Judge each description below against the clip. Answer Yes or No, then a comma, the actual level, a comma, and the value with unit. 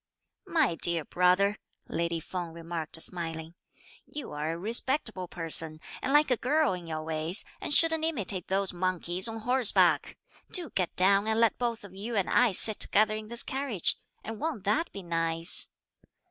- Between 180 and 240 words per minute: No, average, 165 wpm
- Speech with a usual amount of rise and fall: No, wide, 5.8 semitones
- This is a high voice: Yes, high, 195 Hz